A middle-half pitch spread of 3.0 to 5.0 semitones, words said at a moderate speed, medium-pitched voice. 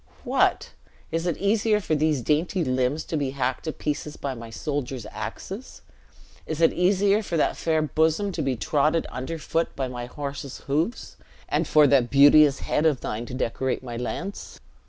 Yes: average, 3.9 semitones; average, 175 wpm; medium, 150 Hz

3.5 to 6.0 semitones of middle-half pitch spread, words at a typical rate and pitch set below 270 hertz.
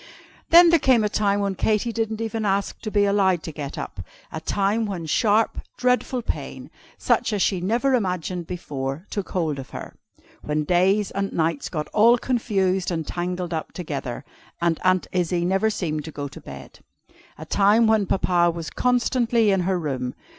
Yes: average, 4.5 semitones; average, 180 wpm; high, 190 Hz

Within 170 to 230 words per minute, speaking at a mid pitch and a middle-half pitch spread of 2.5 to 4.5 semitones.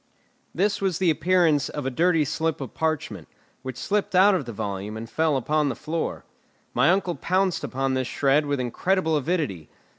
No: average, 180 wpm; medium, 155 Hz; wide, 5.4 semitones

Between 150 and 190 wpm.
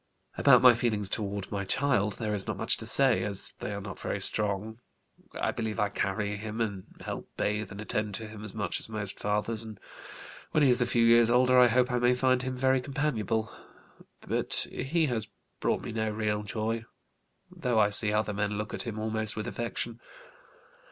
No: average, 200 wpm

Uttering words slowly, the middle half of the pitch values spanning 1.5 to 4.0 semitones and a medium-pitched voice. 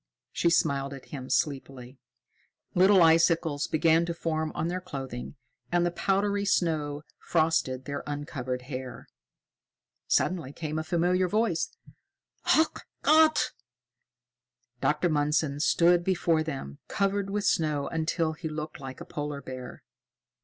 Yes: slow, 125 wpm; average, 3.6 semitones; medium, 155 Hz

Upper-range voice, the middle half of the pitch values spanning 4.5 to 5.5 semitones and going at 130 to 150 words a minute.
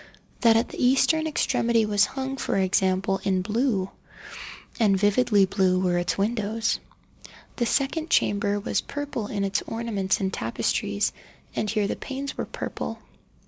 No: high, 210 Hz; average, 3.7 semitones; average, 140 wpm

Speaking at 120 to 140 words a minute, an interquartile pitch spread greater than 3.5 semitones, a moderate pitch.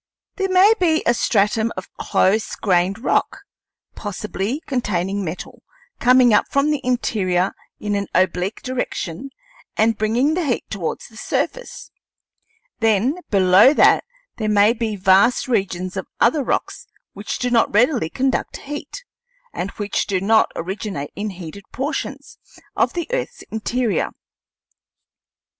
No: slow, 135 wpm; average, 4.7 semitones; high, 215 Hz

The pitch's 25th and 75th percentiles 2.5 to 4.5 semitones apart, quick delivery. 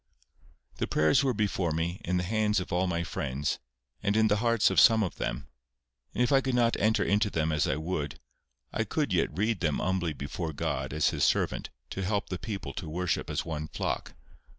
No: average, 5.1 semitones; fast, 210 wpm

